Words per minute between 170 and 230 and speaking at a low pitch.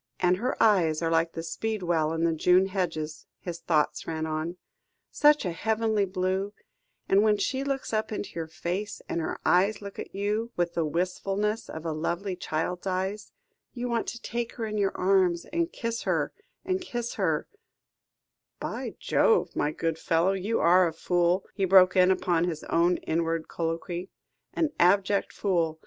No: average, 175 wpm; medium, 185 Hz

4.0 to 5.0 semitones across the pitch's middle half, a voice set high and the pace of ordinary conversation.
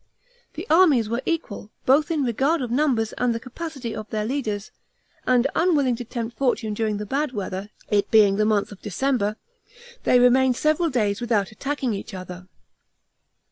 Yes: average, 4.5 semitones; high, 240 Hz; average, 170 wpm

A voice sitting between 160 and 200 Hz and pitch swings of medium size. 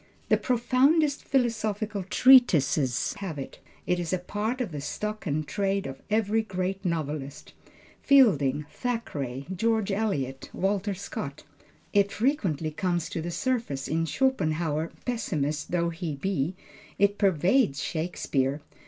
No: medium, 185 Hz; wide, 6.3 semitones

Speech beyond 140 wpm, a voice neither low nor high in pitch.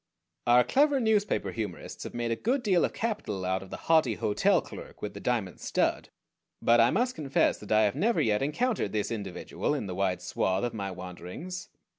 No: average, 200 wpm; low, 115 Hz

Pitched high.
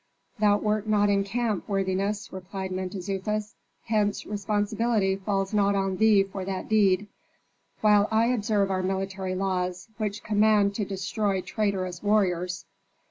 Yes: high, 200 Hz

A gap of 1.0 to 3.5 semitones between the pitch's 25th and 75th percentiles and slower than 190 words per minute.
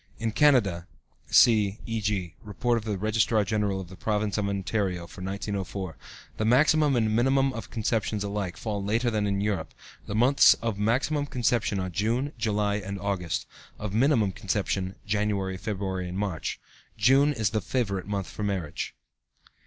Yes: average, 2.7 semitones; average, 160 wpm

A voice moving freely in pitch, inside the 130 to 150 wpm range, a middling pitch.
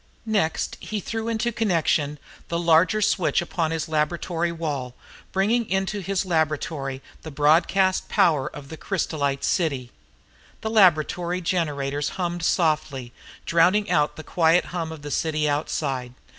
No: average, 3.7 semitones; slow, 135 wpm; medium, 165 Hz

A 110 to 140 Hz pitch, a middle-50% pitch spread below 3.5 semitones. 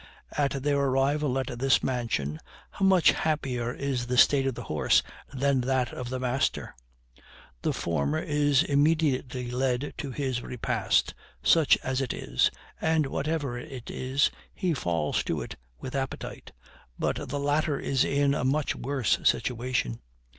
Yes: low, 135 Hz; narrow, 2.4 semitones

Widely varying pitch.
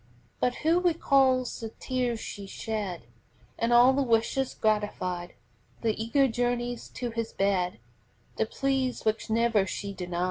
No: average, 3.5 semitones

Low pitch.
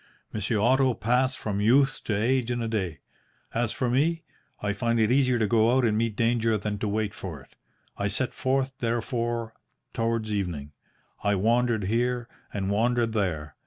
Yes: low, 115 Hz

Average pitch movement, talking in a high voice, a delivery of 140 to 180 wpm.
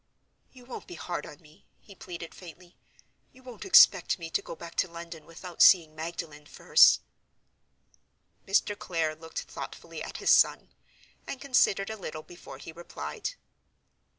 No: average, 3.4 semitones; medium, 170 Hz; average, 150 wpm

